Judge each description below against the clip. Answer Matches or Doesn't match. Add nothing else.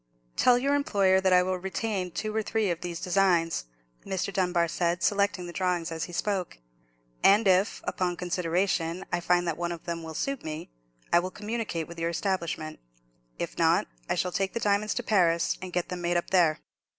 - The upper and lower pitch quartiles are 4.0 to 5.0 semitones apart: Doesn't match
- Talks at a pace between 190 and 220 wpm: Matches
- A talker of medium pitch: Matches